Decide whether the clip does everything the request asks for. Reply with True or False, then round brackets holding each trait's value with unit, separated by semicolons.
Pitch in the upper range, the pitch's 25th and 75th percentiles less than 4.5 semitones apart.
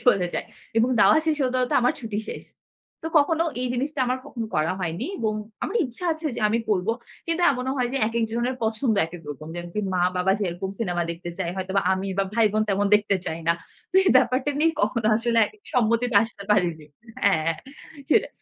False (220 Hz; 5.4 semitones)